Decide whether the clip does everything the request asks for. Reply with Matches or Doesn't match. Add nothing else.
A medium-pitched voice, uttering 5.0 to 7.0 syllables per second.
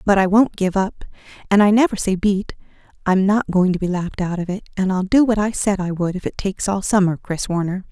Doesn't match